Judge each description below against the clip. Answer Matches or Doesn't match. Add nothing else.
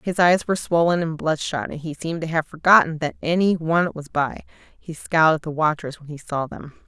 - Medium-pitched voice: Matches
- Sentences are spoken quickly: Matches